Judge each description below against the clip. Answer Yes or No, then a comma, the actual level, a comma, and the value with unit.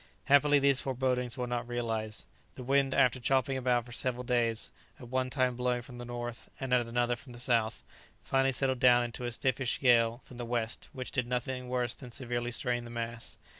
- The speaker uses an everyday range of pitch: No, narrow, 1.3 semitones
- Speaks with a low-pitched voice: Yes, low, 125 Hz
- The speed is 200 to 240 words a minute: Yes, fast, 205 wpm